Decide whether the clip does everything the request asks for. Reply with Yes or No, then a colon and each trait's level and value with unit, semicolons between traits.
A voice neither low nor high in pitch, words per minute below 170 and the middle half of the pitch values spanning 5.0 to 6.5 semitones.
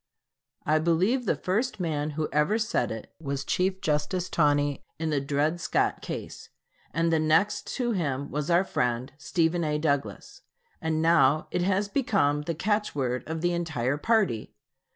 No: medium, 160 Hz; average, 160 wpm; average, 4.0 semitones